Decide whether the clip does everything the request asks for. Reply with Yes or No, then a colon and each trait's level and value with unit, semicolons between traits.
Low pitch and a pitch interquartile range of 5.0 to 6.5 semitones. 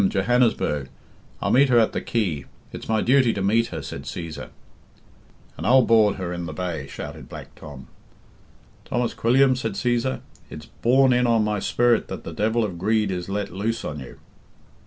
Yes: low, 110 Hz; wide, 5.4 semitones